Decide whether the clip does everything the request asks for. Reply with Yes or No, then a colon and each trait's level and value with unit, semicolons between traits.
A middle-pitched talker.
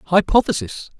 Yes: medium, 170 Hz